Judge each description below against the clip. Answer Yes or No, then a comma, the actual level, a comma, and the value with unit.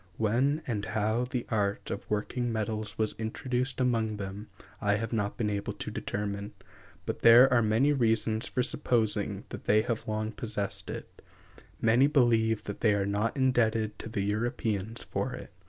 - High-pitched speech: No, low, 110 Hz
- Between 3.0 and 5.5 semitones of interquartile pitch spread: No, narrow, 2.4 semitones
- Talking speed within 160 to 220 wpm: Yes, average, 170 wpm